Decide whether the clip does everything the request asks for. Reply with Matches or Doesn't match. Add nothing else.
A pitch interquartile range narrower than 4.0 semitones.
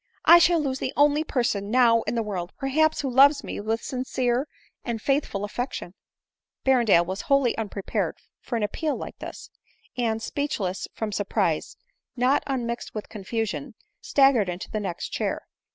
Doesn't match